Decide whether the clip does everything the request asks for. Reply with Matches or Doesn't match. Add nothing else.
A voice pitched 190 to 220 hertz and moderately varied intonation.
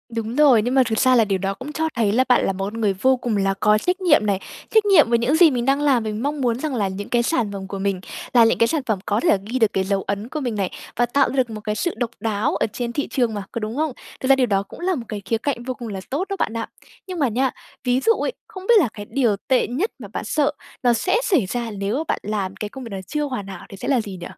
Doesn't match